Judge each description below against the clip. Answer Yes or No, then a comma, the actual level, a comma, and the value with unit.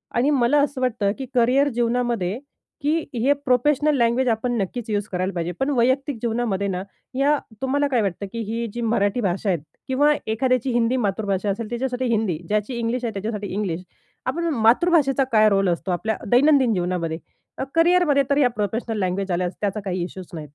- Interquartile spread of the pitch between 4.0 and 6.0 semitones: Yes, average, 4.7 semitones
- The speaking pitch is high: Yes, high, 230 Hz